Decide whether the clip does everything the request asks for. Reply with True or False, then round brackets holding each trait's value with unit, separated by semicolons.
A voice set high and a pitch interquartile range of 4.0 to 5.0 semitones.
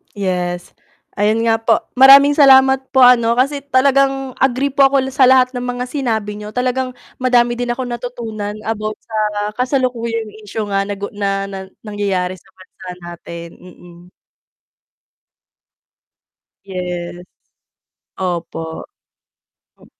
True (230 Hz; 4.7 semitones)